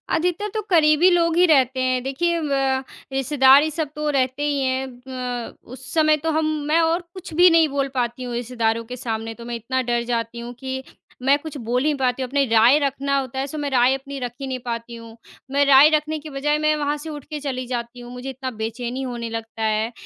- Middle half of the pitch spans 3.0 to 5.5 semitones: Yes, average, 3.6 semitones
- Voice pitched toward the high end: Yes, very high, 265 Hz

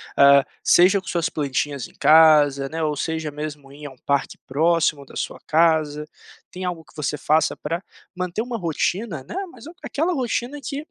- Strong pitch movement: No, average, 3.6 semitones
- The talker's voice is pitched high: No, medium, 155 Hz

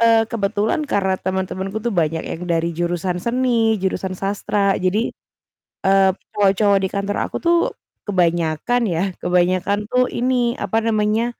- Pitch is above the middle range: Yes, high, 200 Hz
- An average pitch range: Yes, average, 3.6 semitones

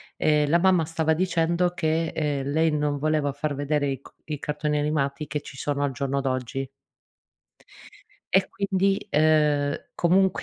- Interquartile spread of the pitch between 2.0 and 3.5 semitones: Yes, narrow, 2.4 semitones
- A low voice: No, medium, 150 Hz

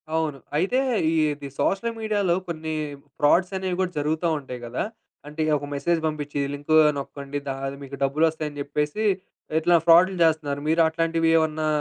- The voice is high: No, medium, 155 Hz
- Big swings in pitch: No, average, 2.8 semitones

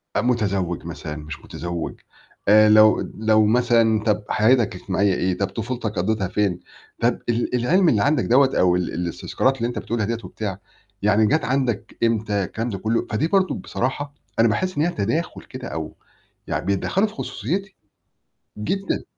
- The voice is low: Yes, low, 110 Hz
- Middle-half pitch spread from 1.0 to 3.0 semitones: No, average, 4.3 semitones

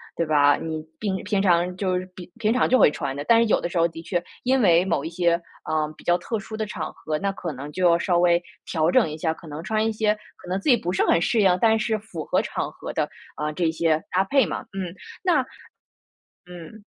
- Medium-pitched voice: Yes, medium, 180 Hz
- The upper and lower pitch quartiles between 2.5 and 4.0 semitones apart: No, average, 4.4 semitones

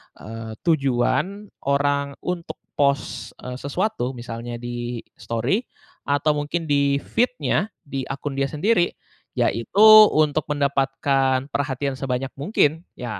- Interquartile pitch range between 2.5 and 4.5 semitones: Yes, average, 3.4 semitones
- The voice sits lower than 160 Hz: Yes, medium, 140 Hz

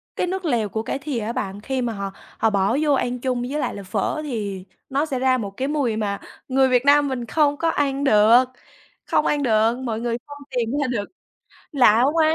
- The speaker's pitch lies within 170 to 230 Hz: No, very high, 250 Hz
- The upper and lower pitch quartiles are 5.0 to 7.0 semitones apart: No, average, 4.4 semitones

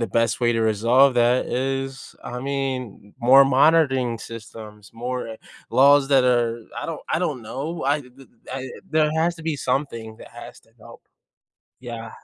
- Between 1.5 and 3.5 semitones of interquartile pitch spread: Yes, average, 3.0 semitones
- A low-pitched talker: Yes, low, 130 Hz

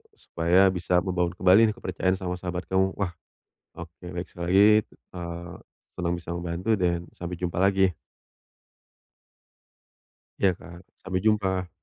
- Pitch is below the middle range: Yes, very low, 90 Hz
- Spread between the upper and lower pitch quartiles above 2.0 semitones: No, narrow, 1.6 semitones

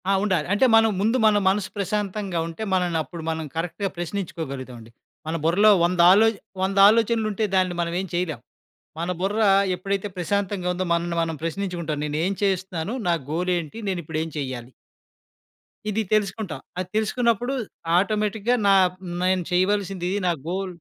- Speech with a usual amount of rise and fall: Yes, average, 3.3 semitones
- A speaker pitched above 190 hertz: No, medium, 185 Hz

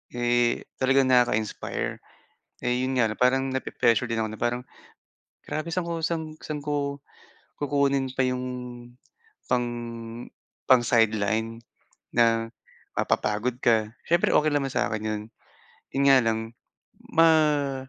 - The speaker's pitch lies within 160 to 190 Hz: No, low, 125 Hz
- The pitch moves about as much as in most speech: Yes, average, 3.7 semitones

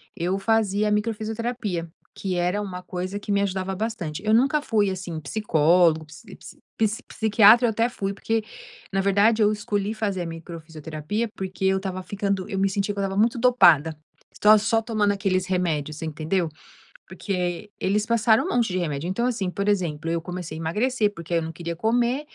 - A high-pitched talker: Yes, high, 195 Hz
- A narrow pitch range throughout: No, average, 3.7 semitones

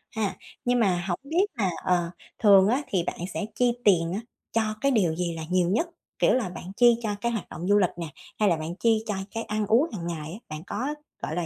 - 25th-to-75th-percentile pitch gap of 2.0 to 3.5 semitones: No, average, 4.7 semitones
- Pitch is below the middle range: No, high, 200 Hz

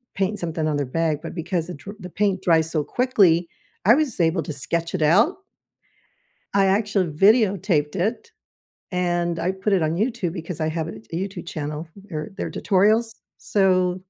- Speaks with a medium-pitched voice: Yes, medium, 180 Hz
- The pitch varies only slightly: No, average, 3.6 semitones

